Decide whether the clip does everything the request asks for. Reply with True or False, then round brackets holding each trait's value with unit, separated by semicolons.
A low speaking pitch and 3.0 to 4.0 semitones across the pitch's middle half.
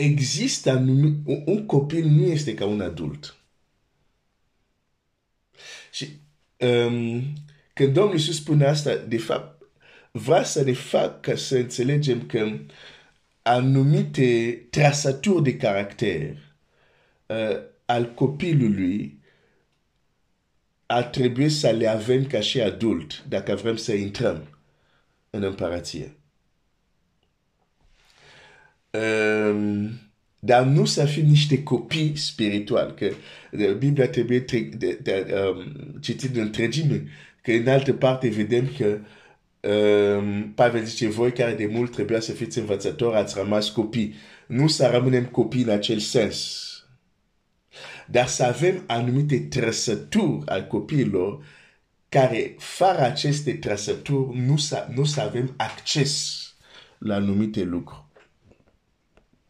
False (120 Hz; 4.8 semitones)